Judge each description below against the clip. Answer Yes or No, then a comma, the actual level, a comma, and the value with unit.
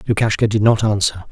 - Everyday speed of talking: Yes, average, 185 wpm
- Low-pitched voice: Yes, low, 105 Hz